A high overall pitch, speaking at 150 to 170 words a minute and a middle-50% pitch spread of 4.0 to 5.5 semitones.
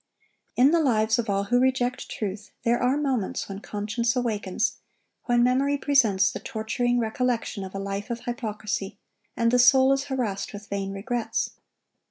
No: high, 235 Hz; average, 165 wpm; average, 3.6 semitones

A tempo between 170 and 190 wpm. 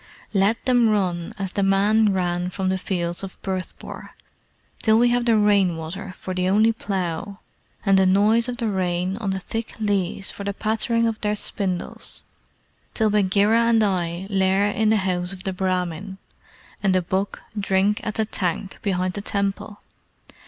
Yes: average, 175 wpm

